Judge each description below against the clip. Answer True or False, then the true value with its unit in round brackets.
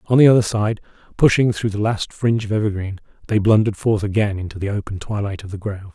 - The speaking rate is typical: False (220 wpm)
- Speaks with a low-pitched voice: True (105 Hz)